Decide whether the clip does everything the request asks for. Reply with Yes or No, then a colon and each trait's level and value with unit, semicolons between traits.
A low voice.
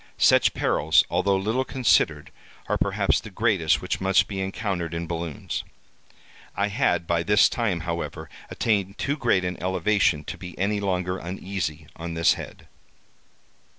Yes: very low, 95 Hz